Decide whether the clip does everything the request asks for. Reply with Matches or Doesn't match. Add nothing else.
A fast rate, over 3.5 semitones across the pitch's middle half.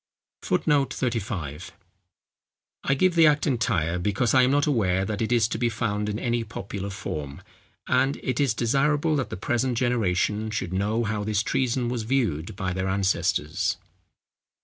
Doesn't match